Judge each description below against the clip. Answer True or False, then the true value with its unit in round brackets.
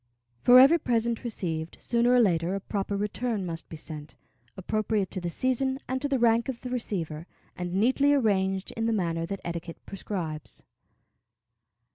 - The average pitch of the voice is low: False (205 Hz)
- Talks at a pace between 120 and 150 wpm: False (165 wpm)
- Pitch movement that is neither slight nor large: False (5.7 semitones)